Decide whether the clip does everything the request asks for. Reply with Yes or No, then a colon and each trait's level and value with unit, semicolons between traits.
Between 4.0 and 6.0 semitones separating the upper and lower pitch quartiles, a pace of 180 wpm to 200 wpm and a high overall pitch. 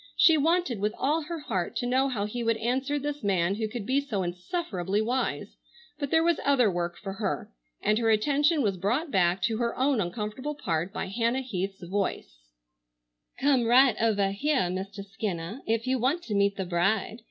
Yes: wide, 5.5 semitones; average, 190 wpm; high, 225 Hz